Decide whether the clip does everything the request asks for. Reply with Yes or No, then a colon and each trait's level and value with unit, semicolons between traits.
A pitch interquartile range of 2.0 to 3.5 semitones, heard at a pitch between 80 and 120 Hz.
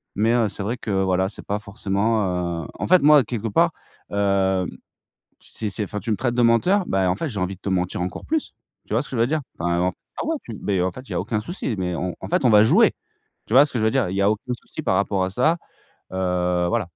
No: average, 4.2 semitones; low, 105 Hz